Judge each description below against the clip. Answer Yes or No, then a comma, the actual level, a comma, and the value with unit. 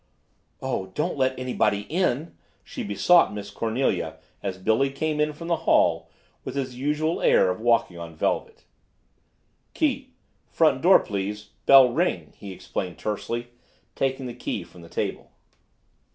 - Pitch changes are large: Yes, wide, 5.9 semitones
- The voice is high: No, low, 120 Hz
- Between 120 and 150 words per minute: Yes, average, 145 wpm